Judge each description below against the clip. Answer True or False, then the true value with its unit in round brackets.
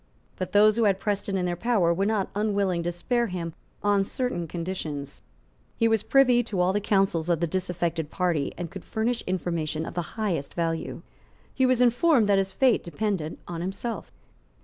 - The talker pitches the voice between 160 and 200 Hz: True (190 Hz)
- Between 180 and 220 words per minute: True (185 wpm)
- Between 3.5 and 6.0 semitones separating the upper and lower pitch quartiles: True (4.1 semitones)